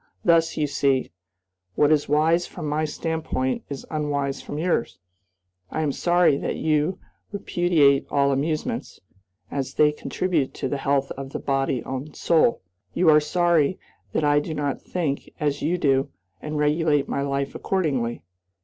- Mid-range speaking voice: Yes, medium, 150 Hz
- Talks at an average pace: Yes, average, 150 wpm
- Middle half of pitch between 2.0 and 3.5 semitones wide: Yes, average, 2.7 semitones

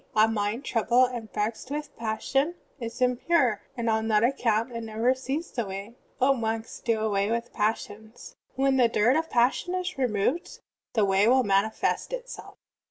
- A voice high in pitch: Yes, high, 230 Hz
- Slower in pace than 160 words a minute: No, average, 170 wpm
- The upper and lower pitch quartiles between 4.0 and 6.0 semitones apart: No, average, 3.1 semitones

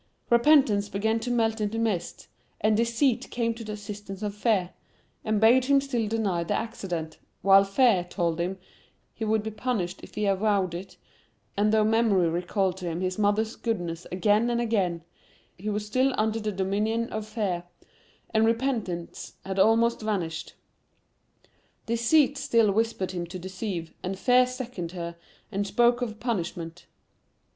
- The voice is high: Yes, high, 210 Hz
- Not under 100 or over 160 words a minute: Yes, average, 155 wpm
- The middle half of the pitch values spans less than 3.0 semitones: No, average, 3.6 semitones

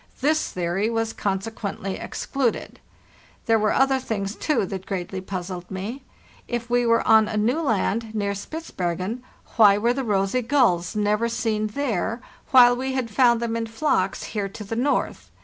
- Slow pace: No, average, 165 wpm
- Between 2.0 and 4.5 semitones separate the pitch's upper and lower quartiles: Yes, average, 3.6 semitones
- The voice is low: No, high, 220 Hz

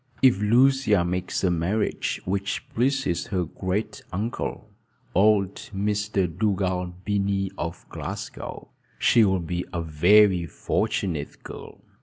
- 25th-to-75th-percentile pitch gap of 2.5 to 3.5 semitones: Yes, average, 2.9 semitones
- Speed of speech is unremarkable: No, slow, 115 wpm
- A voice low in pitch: Yes, very low, 95 Hz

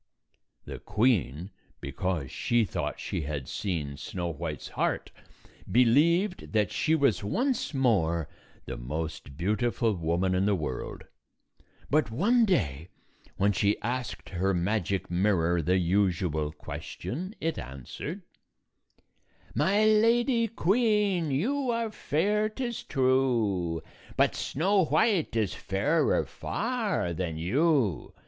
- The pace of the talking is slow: Yes, slow, 120 wpm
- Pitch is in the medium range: No, low, 110 Hz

